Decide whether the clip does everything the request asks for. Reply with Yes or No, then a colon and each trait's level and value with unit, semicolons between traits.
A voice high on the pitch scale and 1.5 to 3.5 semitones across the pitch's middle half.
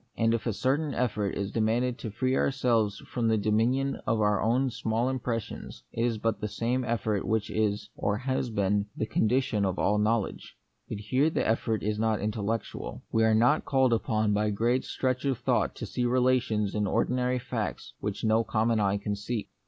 No: low, 110 Hz; average, 3.0 semitones